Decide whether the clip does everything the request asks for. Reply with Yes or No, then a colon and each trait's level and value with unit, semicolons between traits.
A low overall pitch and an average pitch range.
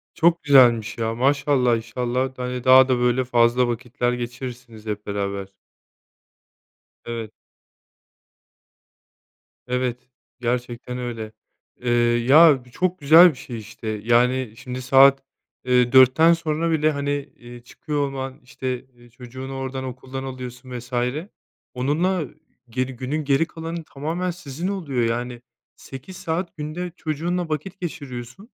Yes: low, 130 Hz; average, 3.6 semitones